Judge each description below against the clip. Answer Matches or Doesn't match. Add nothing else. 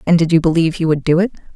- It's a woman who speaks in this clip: Matches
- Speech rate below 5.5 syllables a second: Doesn't match